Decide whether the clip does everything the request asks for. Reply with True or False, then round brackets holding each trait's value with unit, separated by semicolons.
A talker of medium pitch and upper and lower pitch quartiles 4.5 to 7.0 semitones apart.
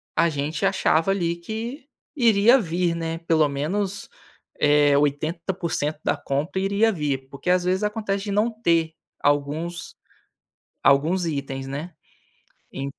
True (170 Hz; 4.9 semitones)